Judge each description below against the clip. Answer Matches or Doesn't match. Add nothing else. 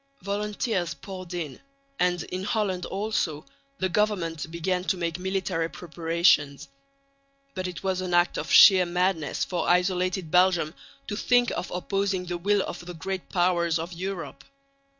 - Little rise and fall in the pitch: Matches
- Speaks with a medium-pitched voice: Matches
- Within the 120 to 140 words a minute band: Doesn't match